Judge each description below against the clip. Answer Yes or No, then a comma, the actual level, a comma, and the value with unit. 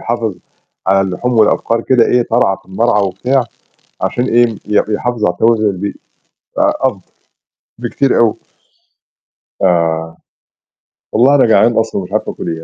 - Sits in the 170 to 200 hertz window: No, low, 110 Hz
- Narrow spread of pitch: No, average, 3.8 semitones